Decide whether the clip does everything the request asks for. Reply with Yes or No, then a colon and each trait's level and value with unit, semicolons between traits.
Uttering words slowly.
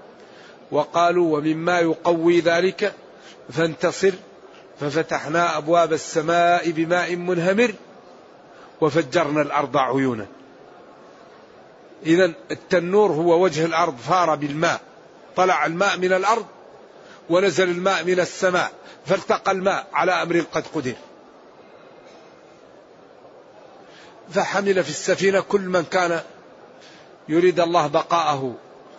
No: average, 90 wpm